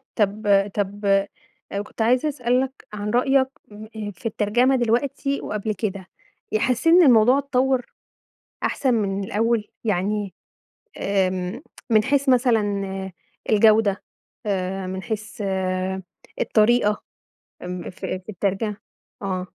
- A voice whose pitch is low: No, high, 215 Hz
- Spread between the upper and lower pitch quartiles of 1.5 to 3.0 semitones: No, average, 3.8 semitones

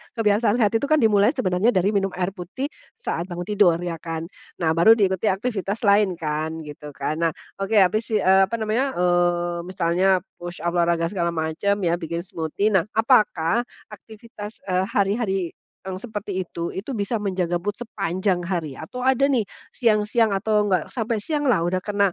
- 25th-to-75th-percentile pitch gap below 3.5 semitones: No, average, 3.8 semitones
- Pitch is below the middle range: No, high, 195 Hz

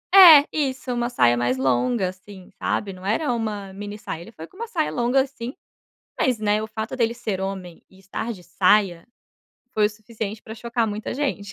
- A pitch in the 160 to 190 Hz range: No, high, 215 Hz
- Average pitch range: Yes, average, 4.1 semitones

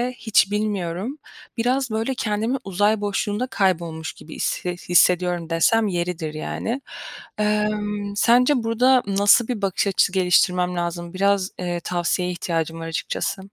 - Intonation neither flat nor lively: Yes, average, 3.7 semitones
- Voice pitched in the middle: No, high, 195 Hz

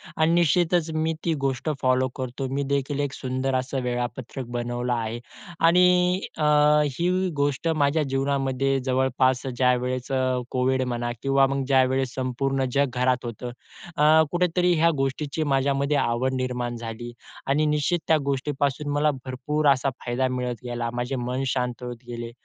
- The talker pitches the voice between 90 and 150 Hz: Yes, low, 135 Hz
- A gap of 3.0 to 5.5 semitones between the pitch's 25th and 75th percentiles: No, narrow, 2.5 semitones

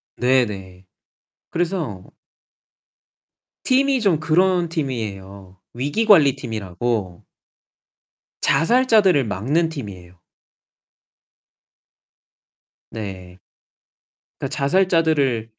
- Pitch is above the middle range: No, low, 135 Hz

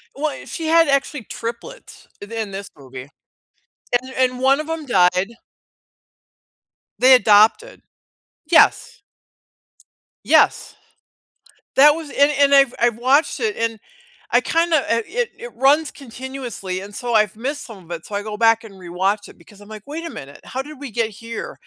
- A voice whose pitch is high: Yes, high, 240 Hz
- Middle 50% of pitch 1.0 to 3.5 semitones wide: No, wide, 5.6 semitones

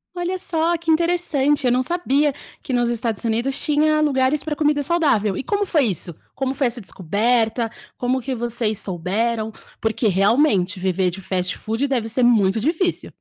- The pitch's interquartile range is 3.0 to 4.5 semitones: No, wide, 5.5 semitones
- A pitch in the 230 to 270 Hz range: Yes, high, 245 Hz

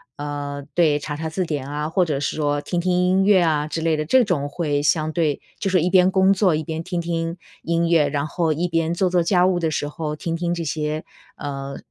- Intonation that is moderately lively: Yes, average, 3.1 semitones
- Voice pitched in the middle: Yes, medium, 165 Hz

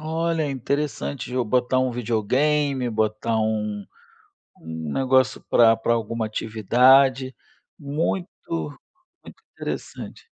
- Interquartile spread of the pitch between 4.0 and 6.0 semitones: Yes, average, 4.3 semitones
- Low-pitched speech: Yes, low, 125 Hz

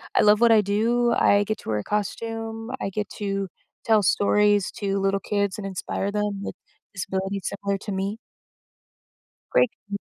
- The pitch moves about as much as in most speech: No, narrow, 1.6 semitones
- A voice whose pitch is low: No, high, 205 Hz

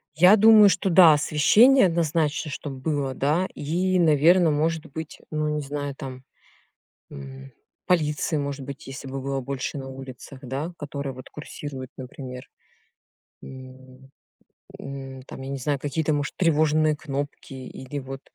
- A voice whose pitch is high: No, medium, 145 Hz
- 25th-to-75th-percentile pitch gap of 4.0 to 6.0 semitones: No, average, 2.9 semitones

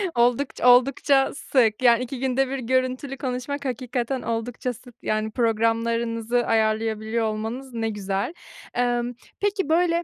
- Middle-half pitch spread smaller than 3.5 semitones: Yes, narrow, 2.6 semitones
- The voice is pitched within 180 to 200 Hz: No, high, 245 Hz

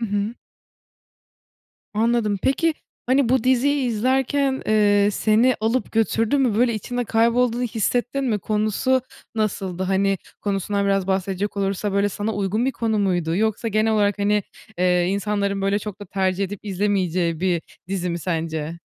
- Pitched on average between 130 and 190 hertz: No, high, 205 Hz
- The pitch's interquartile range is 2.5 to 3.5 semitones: Yes, average, 3.1 semitones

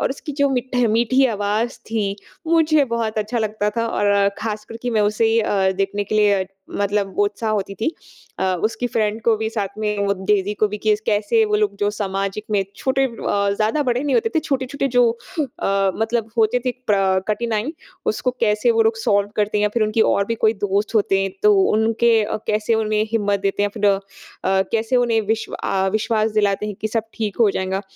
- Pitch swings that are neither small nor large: No, narrow, 2.2 semitones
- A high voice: Yes, high, 215 Hz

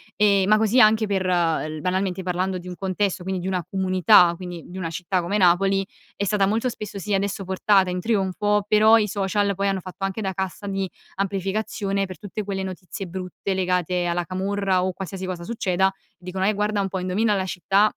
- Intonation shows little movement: Yes, narrow, 1.9 semitones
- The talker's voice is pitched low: No, high, 190 Hz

